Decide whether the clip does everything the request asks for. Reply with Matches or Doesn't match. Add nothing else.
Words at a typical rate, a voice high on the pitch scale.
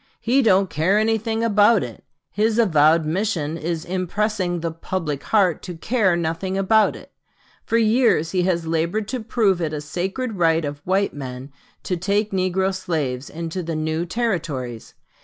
Doesn't match